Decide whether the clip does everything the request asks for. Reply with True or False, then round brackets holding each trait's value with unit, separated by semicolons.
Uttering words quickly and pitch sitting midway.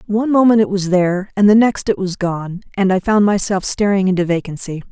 False (220 wpm; 195 Hz)